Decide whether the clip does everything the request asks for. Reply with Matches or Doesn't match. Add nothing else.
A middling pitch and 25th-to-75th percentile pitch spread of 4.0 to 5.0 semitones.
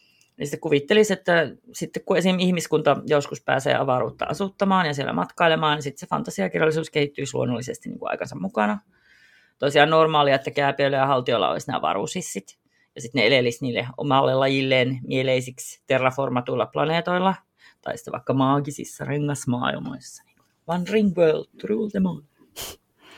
Matches